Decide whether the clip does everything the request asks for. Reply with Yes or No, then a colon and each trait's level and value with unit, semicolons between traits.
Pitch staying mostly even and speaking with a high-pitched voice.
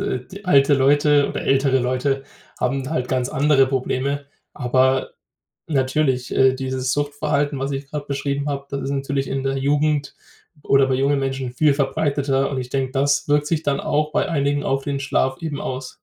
No: narrow, 1.5 semitones; medium, 140 Hz